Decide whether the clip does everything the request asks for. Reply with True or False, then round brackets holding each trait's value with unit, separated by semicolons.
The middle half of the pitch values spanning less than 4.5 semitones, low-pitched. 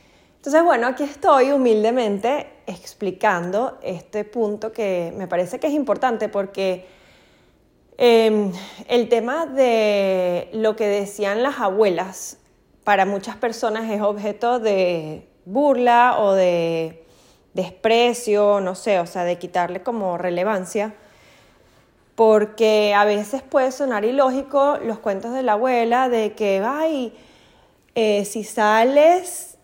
False (3.9 semitones; 215 Hz)